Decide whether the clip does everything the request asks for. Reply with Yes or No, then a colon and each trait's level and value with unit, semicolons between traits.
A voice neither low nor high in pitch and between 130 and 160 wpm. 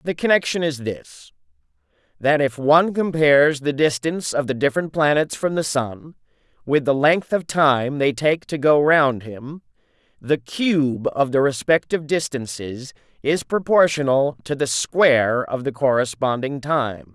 Yes: medium, 145 Hz; average, 150 wpm